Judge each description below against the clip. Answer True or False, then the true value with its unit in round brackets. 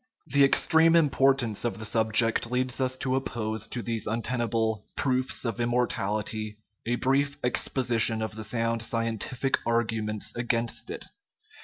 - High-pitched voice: False (115 Hz)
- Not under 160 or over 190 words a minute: False (145 wpm)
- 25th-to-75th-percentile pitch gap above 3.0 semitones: False (2.5 semitones)